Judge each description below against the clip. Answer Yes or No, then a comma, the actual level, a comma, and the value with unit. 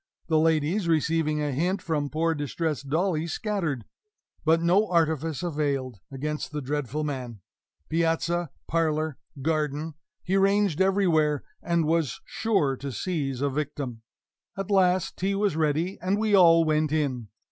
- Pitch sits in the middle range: Yes, medium, 160 Hz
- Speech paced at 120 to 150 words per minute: Yes, average, 140 wpm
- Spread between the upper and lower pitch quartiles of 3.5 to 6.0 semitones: No, average, 2.9 semitones